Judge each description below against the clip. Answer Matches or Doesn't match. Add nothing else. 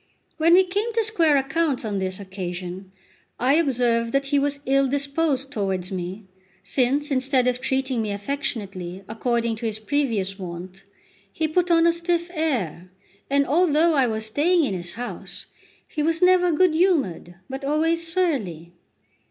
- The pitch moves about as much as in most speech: Doesn't match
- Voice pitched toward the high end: Matches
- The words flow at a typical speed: Matches